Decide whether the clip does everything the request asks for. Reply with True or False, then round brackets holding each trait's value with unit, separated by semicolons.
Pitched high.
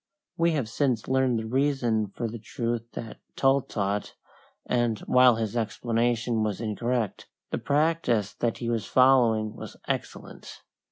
False (120 Hz)